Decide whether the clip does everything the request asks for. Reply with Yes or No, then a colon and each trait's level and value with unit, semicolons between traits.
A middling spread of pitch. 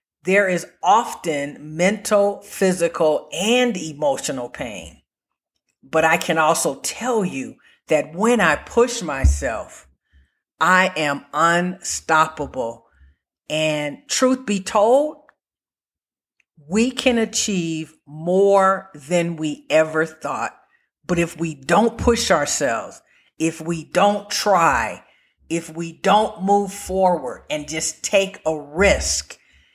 Yes: average, 4.3 semitones